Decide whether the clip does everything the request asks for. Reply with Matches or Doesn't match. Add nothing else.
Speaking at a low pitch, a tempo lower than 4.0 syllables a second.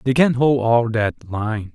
Matches